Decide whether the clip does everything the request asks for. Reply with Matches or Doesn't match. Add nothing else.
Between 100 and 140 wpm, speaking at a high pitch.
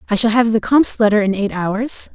Doesn't match